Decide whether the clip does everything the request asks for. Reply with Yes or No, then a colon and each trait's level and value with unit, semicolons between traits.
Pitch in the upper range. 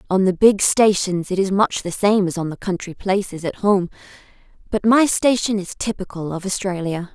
Yes: high, 195 Hz